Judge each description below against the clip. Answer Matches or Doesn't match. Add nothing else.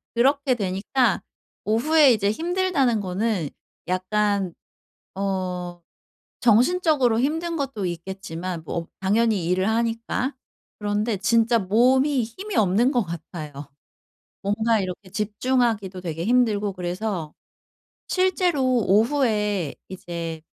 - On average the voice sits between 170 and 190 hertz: Doesn't match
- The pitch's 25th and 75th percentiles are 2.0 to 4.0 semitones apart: Doesn't match